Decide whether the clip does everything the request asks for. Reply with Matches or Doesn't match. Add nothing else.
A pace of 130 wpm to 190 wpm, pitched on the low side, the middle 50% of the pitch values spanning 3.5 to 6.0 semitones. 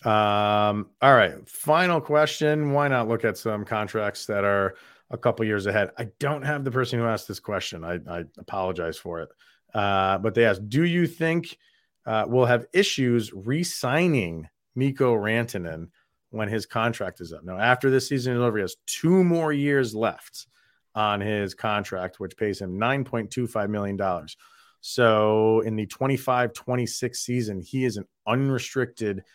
Matches